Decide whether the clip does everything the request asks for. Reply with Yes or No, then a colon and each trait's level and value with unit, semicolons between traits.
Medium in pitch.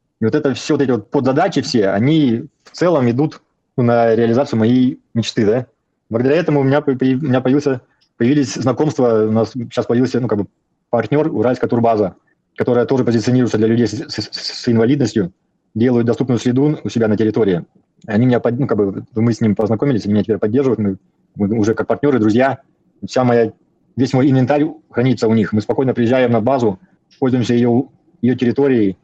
No: low, 120 Hz